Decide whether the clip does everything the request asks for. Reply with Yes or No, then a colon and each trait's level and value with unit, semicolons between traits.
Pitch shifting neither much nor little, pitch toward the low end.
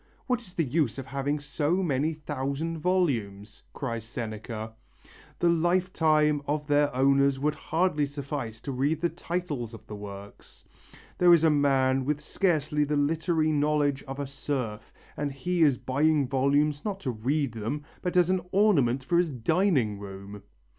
No: average, 3.6 semitones; medium, 145 Hz